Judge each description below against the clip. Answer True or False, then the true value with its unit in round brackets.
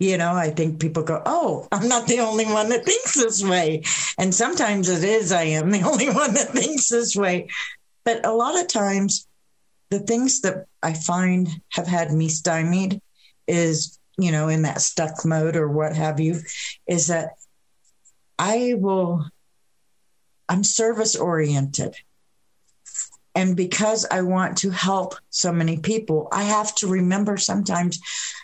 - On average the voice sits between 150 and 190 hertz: True (185 Hz)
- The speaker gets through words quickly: False (160 wpm)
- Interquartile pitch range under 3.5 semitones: False (4.2 semitones)